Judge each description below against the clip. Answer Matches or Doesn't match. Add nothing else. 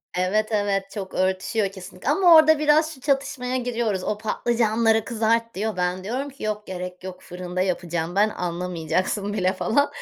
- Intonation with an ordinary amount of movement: Matches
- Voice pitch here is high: Matches